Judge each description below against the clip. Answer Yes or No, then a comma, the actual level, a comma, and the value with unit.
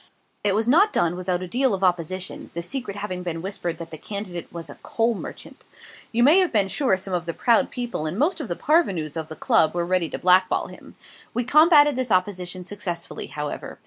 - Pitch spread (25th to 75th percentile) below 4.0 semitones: No, wide, 5.5 semitones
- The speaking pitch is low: No, medium, 185 Hz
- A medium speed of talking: No, fast, 210 wpm